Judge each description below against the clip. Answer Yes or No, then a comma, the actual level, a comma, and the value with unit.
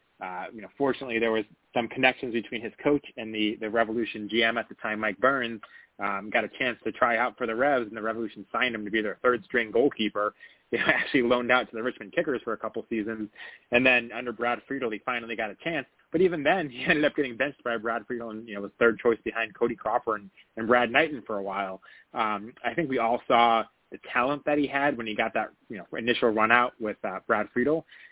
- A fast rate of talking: Yes, fast, 245 wpm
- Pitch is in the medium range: No, low, 115 Hz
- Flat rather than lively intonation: Yes, narrow, 2.1 semitones